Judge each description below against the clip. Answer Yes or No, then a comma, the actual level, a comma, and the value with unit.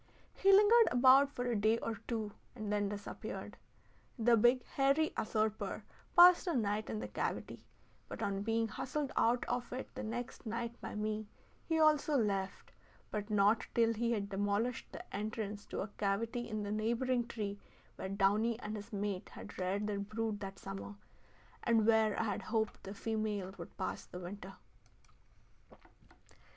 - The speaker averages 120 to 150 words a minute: No, average, 165 wpm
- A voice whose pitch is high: Yes, high, 215 Hz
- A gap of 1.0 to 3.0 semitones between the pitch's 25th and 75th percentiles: Yes, average, 2.7 semitones